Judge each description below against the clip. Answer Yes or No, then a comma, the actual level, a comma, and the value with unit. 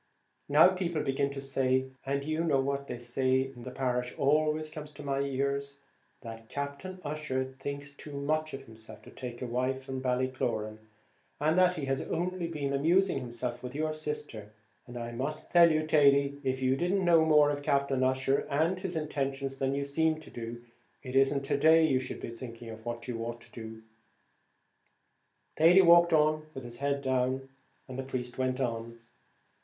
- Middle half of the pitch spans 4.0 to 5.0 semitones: No, average, 3.1 semitones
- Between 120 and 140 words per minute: No, average, 185 wpm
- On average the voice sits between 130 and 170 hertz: Yes, medium, 140 Hz